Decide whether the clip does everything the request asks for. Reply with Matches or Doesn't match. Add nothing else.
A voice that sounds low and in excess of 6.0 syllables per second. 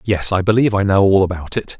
Matches